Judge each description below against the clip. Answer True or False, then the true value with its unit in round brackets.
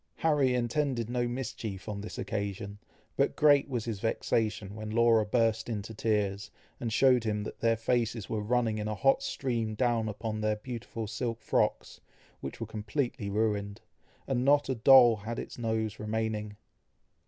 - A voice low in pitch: True (110 Hz)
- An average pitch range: False (2.3 semitones)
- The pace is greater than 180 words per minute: False (165 wpm)